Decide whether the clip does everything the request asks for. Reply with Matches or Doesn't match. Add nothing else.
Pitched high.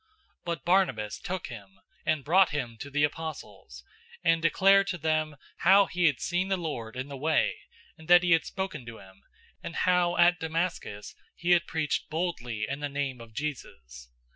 Doesn't match